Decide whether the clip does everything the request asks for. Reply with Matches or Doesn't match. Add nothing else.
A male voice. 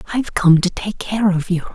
Doesn't match